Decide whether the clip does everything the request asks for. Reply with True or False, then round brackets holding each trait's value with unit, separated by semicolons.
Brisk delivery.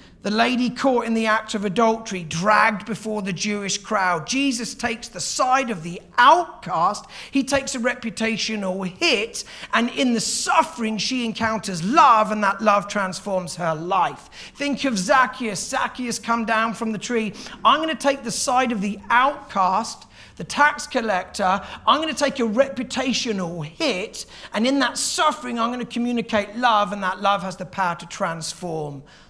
False (170 wpm)